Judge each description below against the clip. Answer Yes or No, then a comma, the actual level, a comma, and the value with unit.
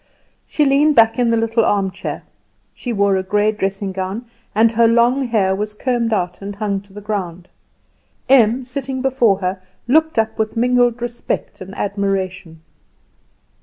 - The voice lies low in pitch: No, high, 215 Hz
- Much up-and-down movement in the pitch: No, average, 3.7 semitones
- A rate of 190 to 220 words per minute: No, average, 160 wpm